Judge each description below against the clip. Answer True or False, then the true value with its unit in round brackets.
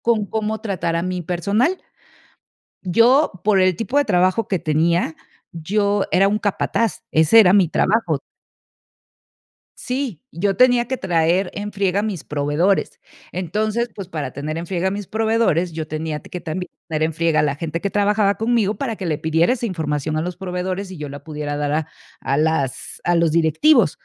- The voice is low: False (180 Hz)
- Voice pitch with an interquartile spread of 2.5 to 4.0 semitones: False (4.7 semitones)